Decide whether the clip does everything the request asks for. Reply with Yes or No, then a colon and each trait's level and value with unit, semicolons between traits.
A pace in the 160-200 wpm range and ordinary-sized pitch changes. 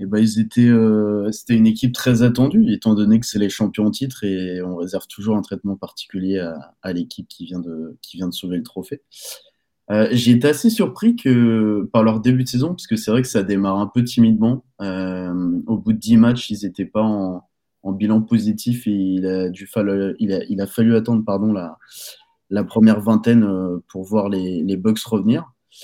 No: fast, 220 wpm; average, 3.2 semitones